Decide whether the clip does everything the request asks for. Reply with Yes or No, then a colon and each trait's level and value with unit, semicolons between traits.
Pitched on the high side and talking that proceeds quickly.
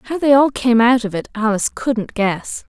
Yes: high, 235 Hz; fast, 220 wpm